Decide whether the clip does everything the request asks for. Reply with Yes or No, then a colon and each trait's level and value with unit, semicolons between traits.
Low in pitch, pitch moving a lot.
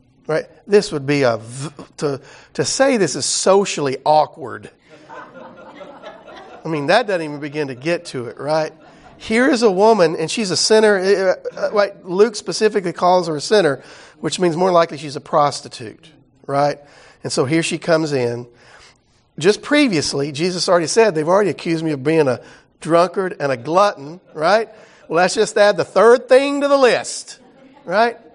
No: medium, 175 Hz; wide, 5.9 semitones